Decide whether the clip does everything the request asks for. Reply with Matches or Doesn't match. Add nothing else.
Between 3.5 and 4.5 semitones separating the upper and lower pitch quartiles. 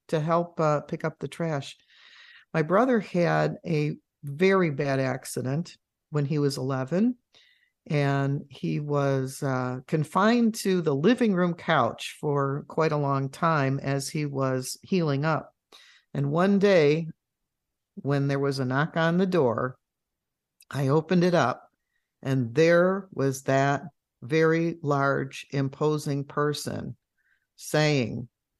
Matches